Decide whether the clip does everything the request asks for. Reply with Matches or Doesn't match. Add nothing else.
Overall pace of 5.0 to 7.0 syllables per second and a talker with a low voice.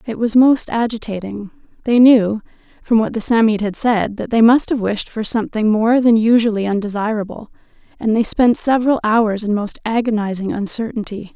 Doesn't match